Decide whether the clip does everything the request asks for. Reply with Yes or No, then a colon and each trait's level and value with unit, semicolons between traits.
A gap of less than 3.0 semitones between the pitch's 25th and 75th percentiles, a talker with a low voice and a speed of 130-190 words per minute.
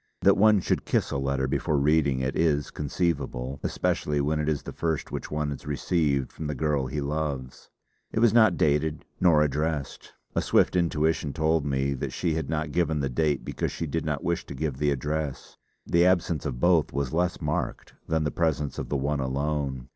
No: narrow, 2.5 semitones; very low, 75 Hz; average, 200 wpm